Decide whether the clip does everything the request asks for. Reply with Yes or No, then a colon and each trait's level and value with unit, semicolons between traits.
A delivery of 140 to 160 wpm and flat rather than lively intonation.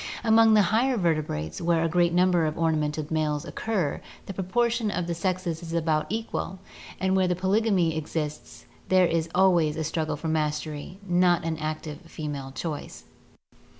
No: average, 155 wpm; average, 3.3 semitones